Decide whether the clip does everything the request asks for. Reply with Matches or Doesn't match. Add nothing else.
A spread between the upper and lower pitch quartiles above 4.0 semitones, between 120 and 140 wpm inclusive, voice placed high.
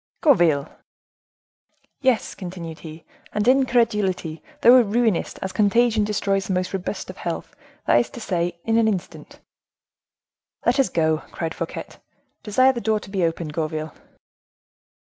Matches